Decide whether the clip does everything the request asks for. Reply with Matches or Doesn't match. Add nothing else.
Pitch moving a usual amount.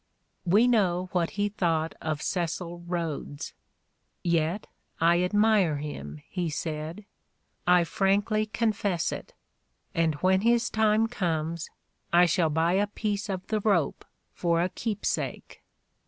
Matches